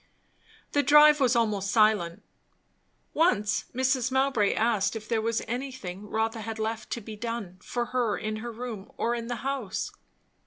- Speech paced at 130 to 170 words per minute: Yes, average, 160 wpm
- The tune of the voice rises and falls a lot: No, average, 2.7 semitones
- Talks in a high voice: Yes, high, 230 Hz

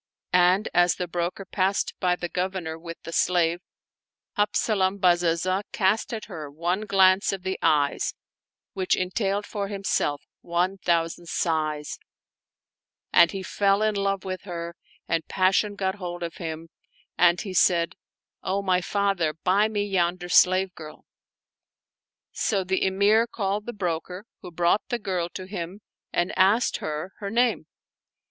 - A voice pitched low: No, medium, 185 Hz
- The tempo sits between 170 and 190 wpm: No, average, 150 wpm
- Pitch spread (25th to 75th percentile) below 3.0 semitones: Yes, narrow, 2.5 semitones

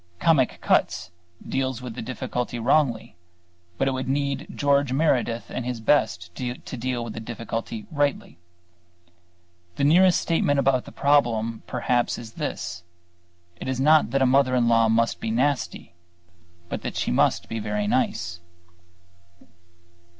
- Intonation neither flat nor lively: Yes, average, 3.4 semitones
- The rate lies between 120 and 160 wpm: Yes, average, 145 wpm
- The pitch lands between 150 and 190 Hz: No, low, 125 Hz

